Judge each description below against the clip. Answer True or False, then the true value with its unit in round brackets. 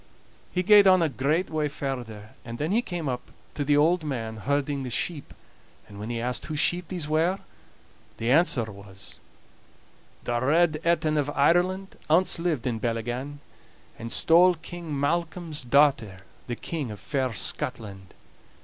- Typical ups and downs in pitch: False (5.9 semitones)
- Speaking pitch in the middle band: True (145 Hz)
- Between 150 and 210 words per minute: True (160 wpm)